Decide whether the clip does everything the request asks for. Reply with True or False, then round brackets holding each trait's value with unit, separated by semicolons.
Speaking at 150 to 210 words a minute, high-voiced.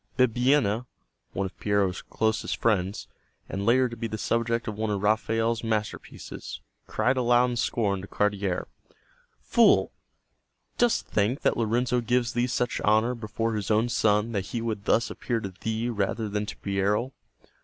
False (160 wpm; 110 Hz)